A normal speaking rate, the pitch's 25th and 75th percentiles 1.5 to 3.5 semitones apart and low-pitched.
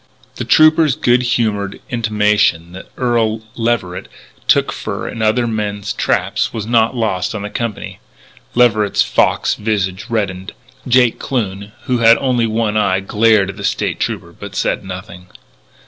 Yes: average, 145 wpm; average, 2.8 semitones; low, 110 Hz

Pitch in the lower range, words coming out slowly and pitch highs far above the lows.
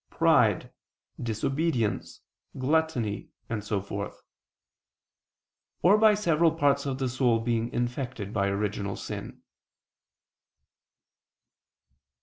Yes: low, 120 Hz; slow, 90 wpm; wide, 5.9 semitones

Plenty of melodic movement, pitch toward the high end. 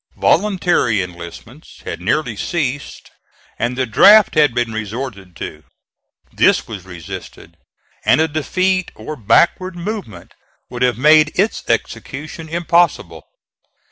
No: wide, 7.6 semitones; medium, 140 Hz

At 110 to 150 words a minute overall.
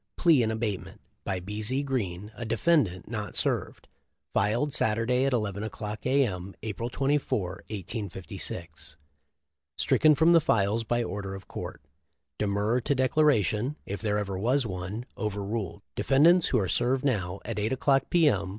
No: average, 160 wpm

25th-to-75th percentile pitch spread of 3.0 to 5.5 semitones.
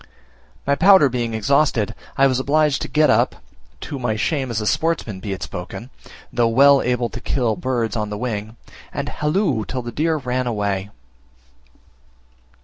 Yes: average, 4.3 semitones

